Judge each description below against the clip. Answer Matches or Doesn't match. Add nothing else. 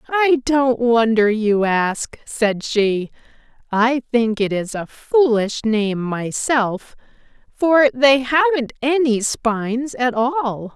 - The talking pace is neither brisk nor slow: Doesn't match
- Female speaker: Matches